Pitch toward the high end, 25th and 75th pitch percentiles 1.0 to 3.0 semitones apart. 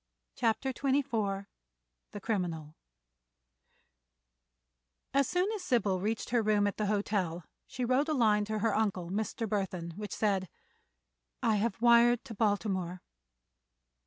No: high, 215 Hz; average, 3.4 semitones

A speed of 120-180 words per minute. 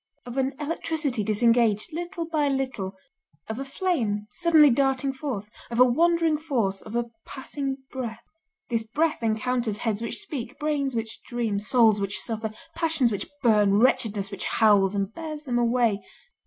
Yes: average, 155 wpm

